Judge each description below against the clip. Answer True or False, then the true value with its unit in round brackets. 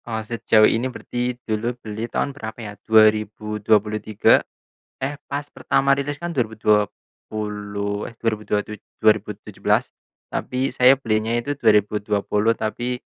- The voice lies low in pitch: True (110 Hz)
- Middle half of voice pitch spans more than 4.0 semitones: False (2.6 semitones)